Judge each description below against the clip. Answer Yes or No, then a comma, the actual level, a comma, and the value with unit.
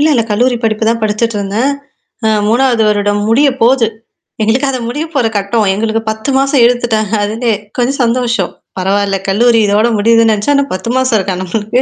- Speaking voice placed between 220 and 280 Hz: Yes, high, 225 Hz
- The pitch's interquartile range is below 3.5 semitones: Yes, average, 3.0 semitones